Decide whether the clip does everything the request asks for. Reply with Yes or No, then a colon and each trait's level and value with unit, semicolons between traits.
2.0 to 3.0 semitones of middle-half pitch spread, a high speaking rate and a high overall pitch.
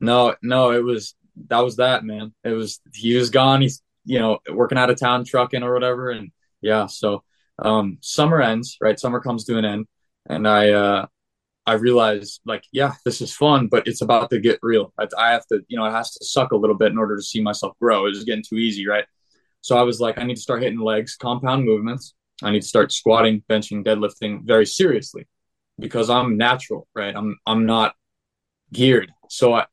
No: narrow, 2.4 semitones; fast, 215 wpm; low, 115 Hz